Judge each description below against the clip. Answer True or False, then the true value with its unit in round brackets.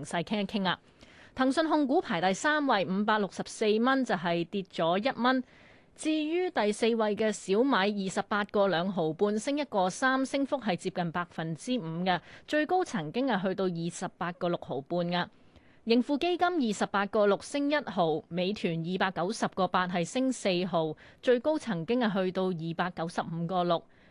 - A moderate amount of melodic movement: False (6.0 semitones)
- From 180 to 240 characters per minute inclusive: False (265 characters per minute)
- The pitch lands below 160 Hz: False (200 Hz)